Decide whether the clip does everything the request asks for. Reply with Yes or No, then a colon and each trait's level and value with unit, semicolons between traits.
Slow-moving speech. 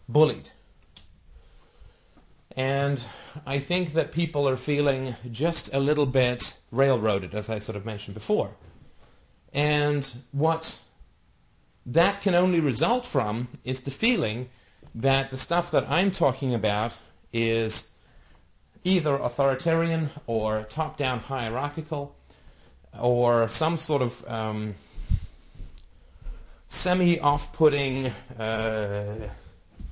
Yes: slow, 100 wpm